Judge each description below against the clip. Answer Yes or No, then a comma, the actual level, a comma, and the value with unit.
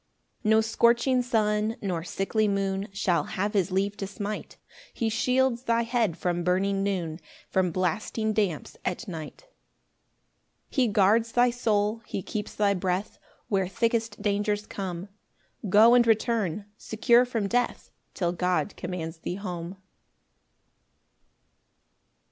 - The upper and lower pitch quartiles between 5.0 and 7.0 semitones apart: No, average, 3.4 semitones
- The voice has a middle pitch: No, high, 205 Hz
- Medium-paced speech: No, slow, 130 wpm